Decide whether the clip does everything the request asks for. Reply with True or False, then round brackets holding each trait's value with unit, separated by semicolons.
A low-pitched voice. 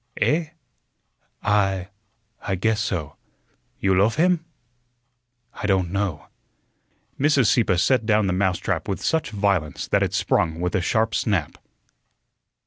True (100 Hz)